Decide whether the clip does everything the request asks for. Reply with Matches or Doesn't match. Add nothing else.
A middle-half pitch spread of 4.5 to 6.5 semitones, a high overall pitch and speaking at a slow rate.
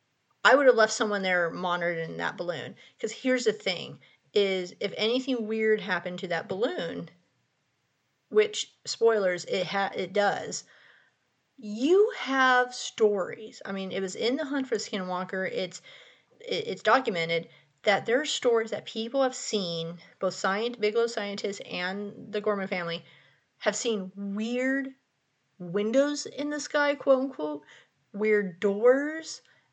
Doesn't match